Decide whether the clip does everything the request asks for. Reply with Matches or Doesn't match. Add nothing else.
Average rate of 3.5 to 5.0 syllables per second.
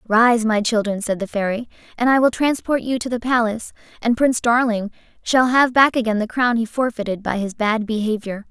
Doesn't match